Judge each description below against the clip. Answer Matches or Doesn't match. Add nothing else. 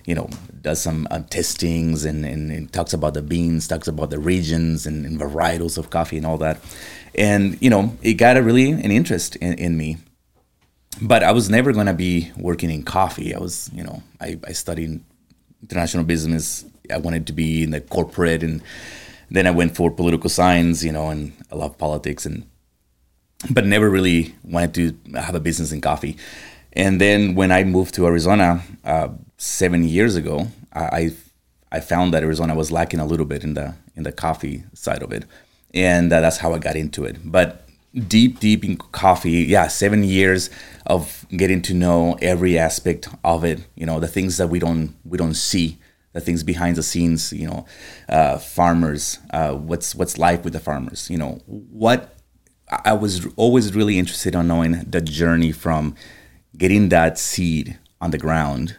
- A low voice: Matches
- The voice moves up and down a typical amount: Doesn't match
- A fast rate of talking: Doesn't match